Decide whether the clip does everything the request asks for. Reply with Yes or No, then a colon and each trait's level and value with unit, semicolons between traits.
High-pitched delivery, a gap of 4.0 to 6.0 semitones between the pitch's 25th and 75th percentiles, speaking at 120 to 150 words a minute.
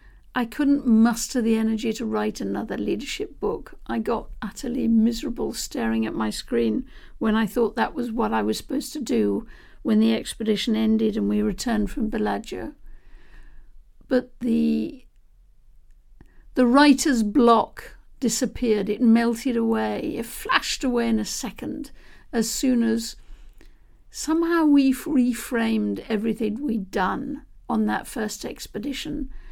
No: high, 235 Hz; average, 2.9 semitones; slow, 135 wpm